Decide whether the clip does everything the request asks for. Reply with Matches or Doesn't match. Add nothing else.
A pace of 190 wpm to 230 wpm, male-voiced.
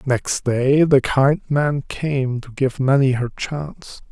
Doesn't match